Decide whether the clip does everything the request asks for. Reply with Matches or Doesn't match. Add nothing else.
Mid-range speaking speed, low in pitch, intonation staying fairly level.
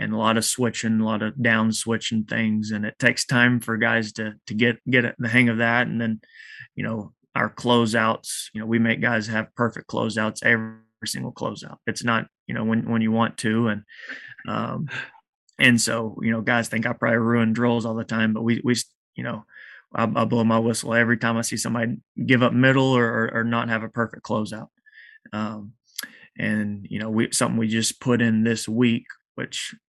Doesn't match